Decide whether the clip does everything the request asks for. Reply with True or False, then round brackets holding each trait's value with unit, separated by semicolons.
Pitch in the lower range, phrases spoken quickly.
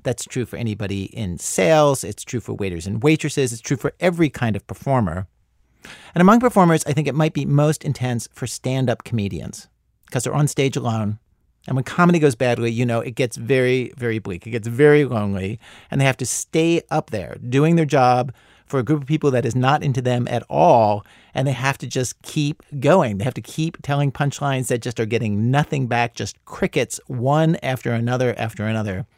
True (130 Hz; 210 wpm)